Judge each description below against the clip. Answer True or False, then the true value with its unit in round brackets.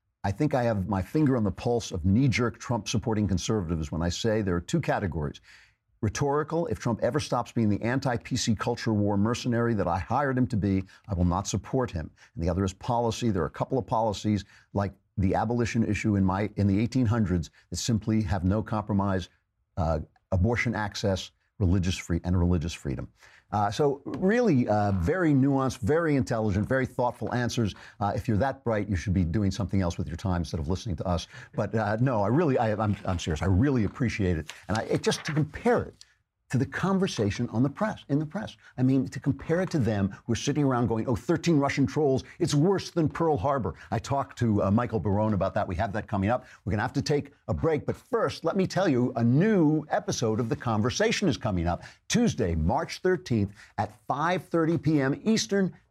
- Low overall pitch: True (110 Hz)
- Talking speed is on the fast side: True (210 wpm)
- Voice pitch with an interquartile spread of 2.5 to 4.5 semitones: False (5.6 semitones)